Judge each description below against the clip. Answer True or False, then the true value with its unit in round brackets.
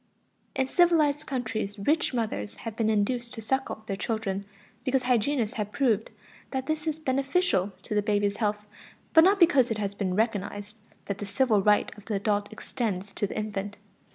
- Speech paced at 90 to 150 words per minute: False (180 wpm)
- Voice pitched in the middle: False (220 Hz)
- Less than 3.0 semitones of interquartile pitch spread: False (4.5 semitones)